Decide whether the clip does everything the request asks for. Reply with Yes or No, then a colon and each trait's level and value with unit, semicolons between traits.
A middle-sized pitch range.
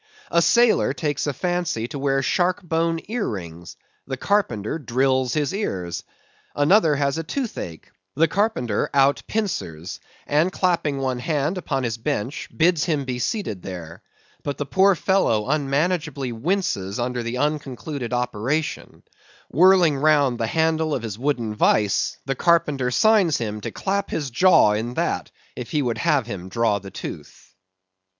No: wide, 6.1 semitones